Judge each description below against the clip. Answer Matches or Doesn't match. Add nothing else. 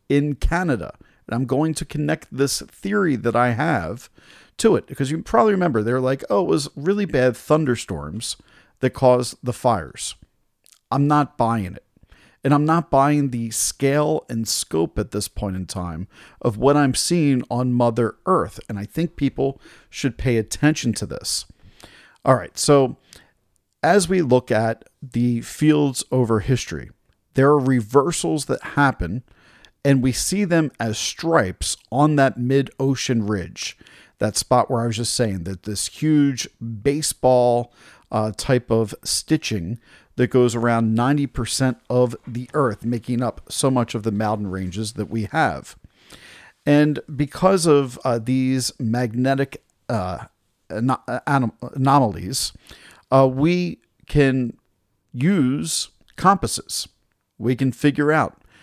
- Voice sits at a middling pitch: Doesn't match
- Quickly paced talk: Doesn't match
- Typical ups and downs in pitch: Matches